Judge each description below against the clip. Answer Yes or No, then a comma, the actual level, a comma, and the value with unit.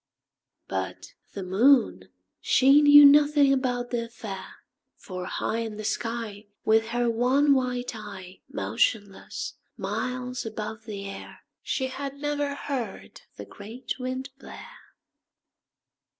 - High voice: Yes, high, 240 Hz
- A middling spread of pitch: Yes, average, 4.3 semitones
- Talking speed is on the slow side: Yes, slow, 120 wpm